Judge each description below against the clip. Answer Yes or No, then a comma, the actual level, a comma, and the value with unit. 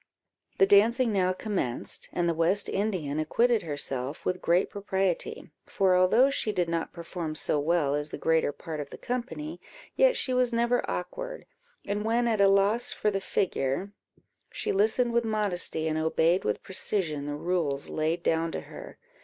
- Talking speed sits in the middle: Yes, average, 170 wpm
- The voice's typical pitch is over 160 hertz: Yes, medium, 185 Hz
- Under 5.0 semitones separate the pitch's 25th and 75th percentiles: No, average, 5.3 semitones